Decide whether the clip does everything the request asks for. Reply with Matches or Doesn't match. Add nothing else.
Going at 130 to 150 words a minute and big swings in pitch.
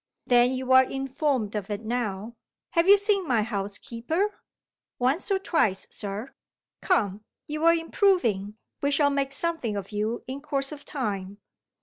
Matches